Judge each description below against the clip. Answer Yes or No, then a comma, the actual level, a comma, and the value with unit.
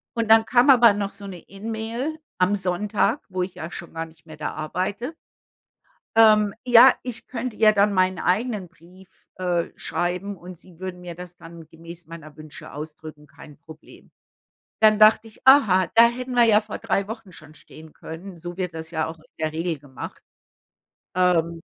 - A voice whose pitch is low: No, medium, 185 Hz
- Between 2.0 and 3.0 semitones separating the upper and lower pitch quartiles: No, average, 4.7 semitones